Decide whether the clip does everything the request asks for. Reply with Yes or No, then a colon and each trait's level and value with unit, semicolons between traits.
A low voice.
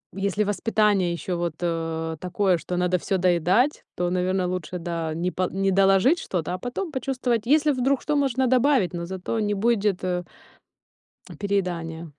No: high, 190 Hz